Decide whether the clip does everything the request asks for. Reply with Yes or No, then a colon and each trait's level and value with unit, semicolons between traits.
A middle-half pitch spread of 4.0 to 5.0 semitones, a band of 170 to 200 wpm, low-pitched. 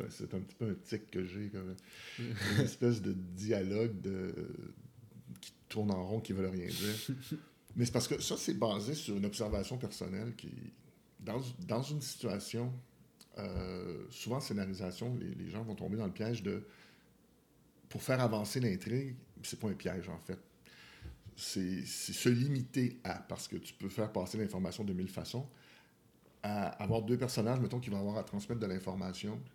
Yes: average, 4.4 semitones; average, 180 wpm; low, 105 Hz